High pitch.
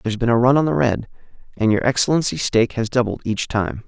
No: low, 115 Hz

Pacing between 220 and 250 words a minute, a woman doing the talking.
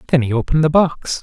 No: fast, 245 wpm; male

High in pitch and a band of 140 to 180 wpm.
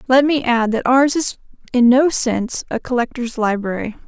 Yes: very high, 250 Hz; average, 175 wpm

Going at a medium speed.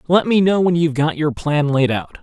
No: fast, 270 wpm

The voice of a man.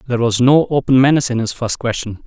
Yes: male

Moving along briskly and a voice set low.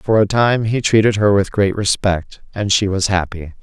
Yes: fast, 215 wpm; low, 100 Hz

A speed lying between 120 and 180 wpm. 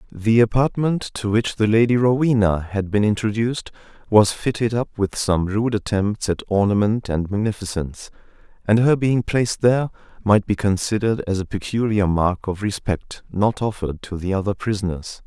Yes: average, 160 wpm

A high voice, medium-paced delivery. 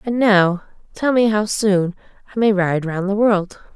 Yes: high, 200 Hz; average, 190 wpm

